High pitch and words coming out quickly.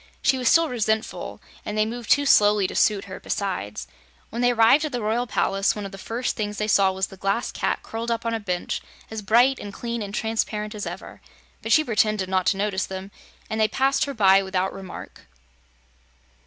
Yes: high, 215 Hz; fast, 210 wpm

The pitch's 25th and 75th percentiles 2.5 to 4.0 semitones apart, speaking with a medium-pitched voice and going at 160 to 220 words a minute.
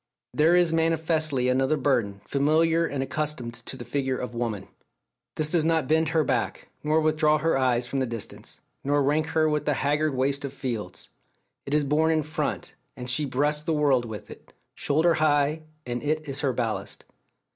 Yes: average, 3.1 semitones; medium, 145 Hz; average, 185 wpm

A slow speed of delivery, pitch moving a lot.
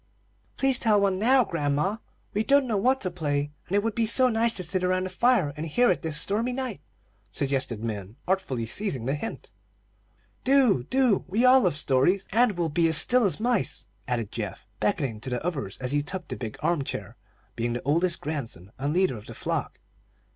No: fast, 205 wpm; wide, 8.0 semitones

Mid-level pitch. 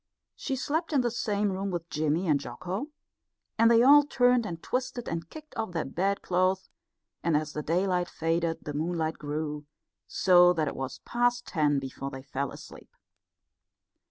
Yes: medium, 175 Hz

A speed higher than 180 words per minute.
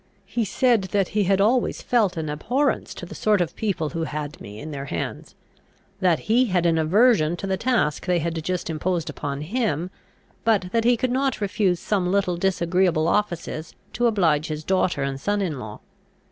Yes: average, 190 wpm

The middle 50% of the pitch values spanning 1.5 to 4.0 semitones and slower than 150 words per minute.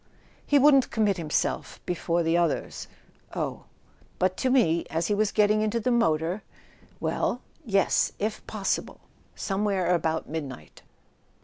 No: average, 4.5 semitones; average, 140 wpm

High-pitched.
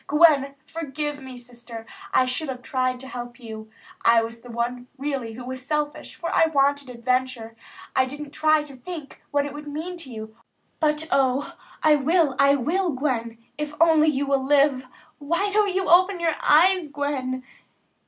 Yes: very high, 280 Hz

